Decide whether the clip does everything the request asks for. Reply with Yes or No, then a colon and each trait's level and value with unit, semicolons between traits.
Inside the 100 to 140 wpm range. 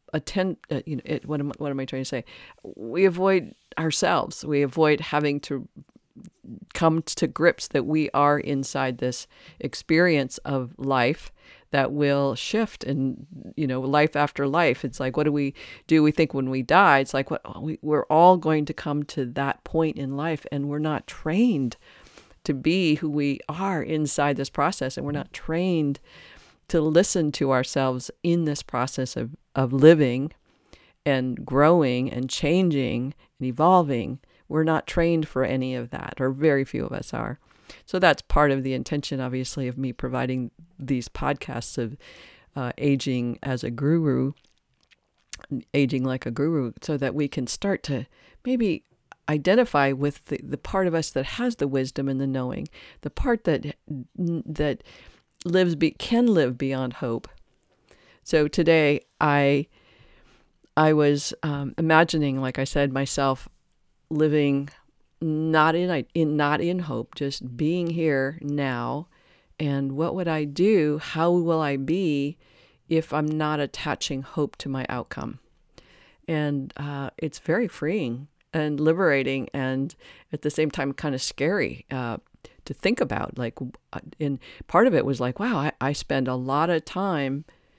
No: average, 160 wpm